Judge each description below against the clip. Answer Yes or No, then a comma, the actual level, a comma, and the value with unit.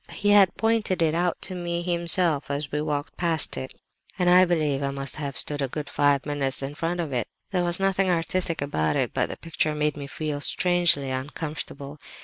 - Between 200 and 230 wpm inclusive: Yes, fast, 205 wpm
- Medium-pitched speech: Yes, medium, 155 Hz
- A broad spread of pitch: No, average, 3.7 semitones